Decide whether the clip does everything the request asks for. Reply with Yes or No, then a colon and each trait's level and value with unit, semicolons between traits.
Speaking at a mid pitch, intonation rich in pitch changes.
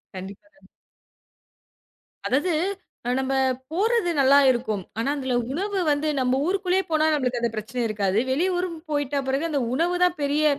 No: very high, 285 Hz; wide, 5.9 semitones